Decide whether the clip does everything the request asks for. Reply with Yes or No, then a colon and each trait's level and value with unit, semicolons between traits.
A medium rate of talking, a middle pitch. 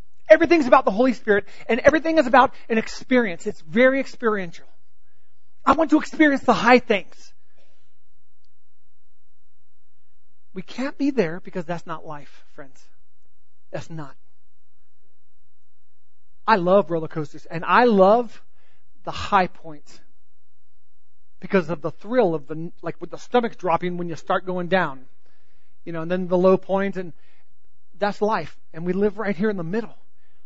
Yes: average, 150 wpm; medium, 165 Hz